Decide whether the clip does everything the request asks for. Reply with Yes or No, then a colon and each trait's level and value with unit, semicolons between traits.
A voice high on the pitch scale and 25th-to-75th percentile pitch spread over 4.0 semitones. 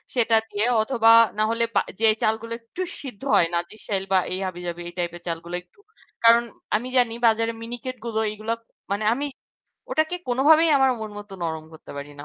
Yes: high, 220 Hz; average, 5.2 semitones